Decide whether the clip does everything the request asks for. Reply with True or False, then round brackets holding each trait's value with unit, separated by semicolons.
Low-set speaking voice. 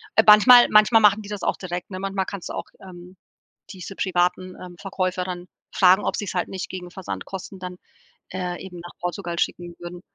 False (185 Hz)